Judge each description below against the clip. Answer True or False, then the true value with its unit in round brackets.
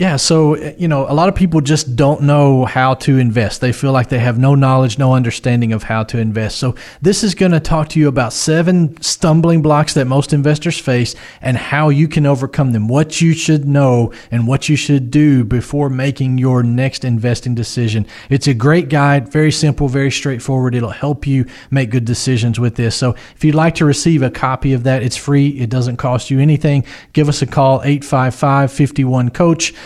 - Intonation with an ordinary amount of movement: True (3.1 semitones)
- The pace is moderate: False (210 wpm)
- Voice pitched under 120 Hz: False (135 Hz)